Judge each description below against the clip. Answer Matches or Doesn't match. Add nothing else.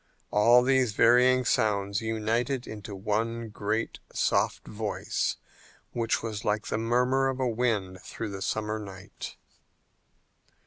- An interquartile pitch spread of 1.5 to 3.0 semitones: Matches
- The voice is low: Matches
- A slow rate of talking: Matches